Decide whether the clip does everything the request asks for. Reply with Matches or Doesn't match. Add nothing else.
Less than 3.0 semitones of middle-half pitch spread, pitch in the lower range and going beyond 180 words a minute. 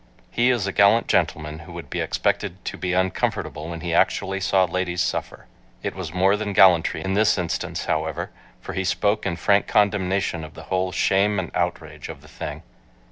Matches